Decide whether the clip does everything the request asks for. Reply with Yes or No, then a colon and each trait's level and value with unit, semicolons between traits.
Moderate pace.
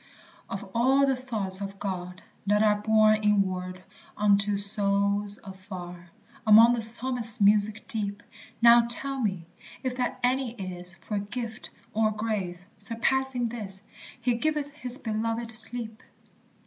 No: slow, 130 wpm